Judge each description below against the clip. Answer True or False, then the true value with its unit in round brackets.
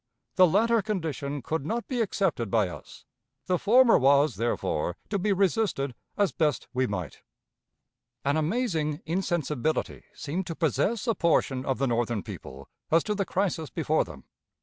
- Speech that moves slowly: False (155 wpm)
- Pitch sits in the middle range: True (160 Hz)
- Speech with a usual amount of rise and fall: False (6.6 semitones)